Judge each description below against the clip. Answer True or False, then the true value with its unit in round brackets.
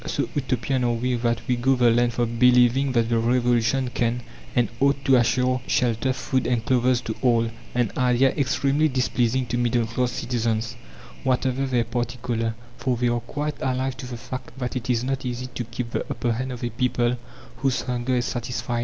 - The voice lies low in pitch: True (125 Hz)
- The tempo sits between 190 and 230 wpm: True (200 wpm)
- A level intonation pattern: True (1.4 semitones)